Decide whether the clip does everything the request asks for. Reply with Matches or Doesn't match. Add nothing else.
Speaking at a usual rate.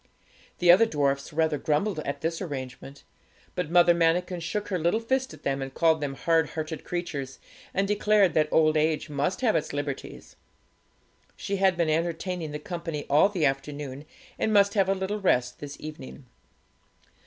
Matches